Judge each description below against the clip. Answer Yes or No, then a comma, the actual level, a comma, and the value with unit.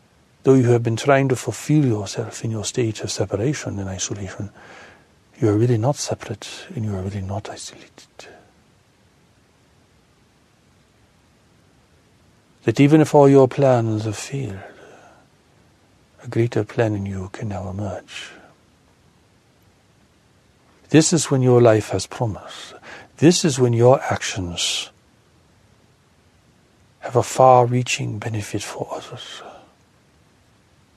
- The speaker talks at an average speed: No, slow, 120 wpm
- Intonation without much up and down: No, average, 4.2 semitones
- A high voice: No, low, 115 Hz